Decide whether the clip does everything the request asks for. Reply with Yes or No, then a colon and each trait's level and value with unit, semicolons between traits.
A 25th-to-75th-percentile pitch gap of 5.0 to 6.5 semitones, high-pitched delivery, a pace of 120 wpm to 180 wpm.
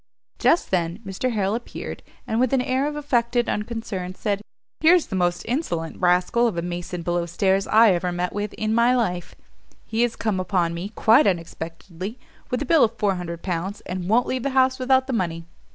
No: average, 5.3 semitones; high, 205 Hz; average, 195 wpm